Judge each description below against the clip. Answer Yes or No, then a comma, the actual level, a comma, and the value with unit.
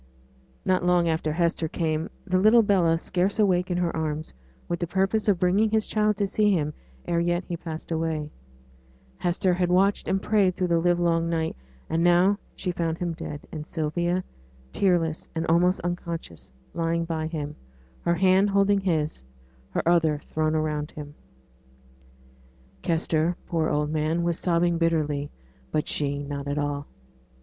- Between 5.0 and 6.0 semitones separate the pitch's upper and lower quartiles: No, narrow, 2.5 semitones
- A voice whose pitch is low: No, medium, 170 Hz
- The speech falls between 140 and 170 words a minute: Yes, average, 160 wpm